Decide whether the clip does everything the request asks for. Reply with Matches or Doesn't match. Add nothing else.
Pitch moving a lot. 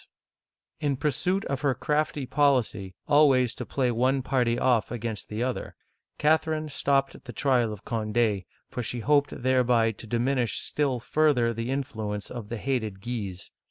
Doesn't match